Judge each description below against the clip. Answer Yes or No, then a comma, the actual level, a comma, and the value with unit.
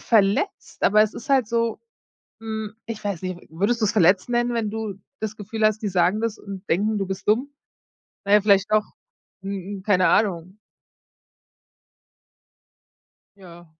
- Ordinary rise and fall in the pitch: No, narrow, 2.3 semitones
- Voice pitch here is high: Yes, high, 210 Hz